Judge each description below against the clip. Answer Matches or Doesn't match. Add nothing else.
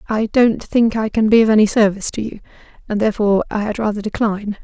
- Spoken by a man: Doesn't match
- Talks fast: Matches